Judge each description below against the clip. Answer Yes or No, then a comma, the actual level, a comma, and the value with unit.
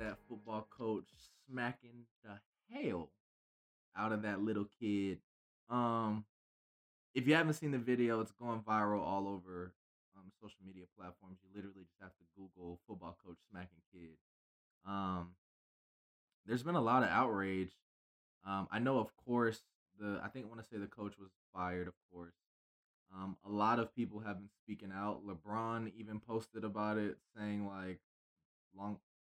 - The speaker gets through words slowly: No, average, 160 wpm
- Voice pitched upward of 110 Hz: No, low, 100 Hz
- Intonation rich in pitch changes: No, average, 3.1 semitones